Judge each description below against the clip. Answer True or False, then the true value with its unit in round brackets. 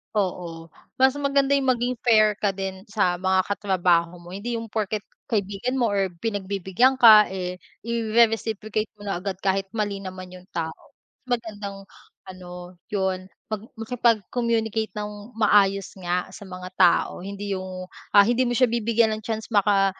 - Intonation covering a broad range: False (3.1 semitones)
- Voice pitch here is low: False (205 Hz)